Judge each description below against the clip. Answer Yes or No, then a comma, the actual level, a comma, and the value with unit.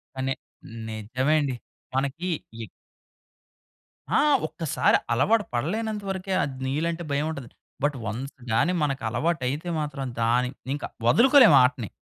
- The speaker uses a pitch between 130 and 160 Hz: Yes, medium, 140 Hz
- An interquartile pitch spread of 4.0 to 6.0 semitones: Yes, average, 5.0 semitones